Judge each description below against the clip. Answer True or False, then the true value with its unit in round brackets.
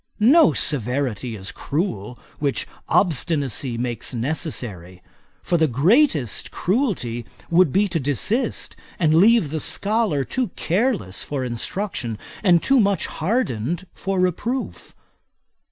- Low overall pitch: False (155 Hz)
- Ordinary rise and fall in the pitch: False (8.1 semitones)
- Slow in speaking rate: True (115 wpm)